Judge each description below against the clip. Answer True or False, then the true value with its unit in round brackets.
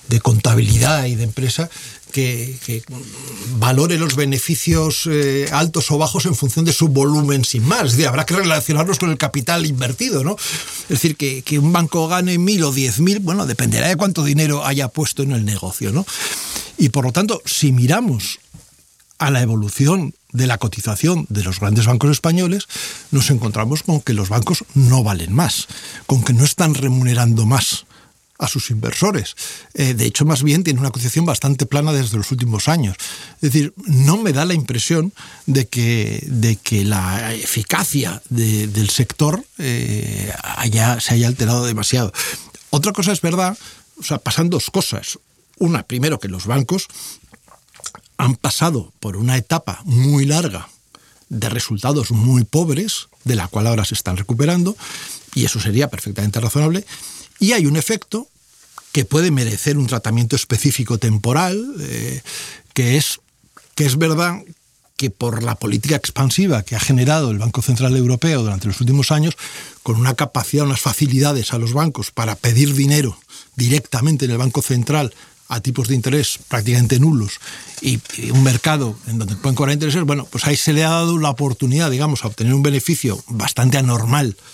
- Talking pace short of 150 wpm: False (170 wpm)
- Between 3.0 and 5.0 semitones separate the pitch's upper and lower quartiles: True (4.4 semitones)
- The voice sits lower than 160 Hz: True (135 Hz)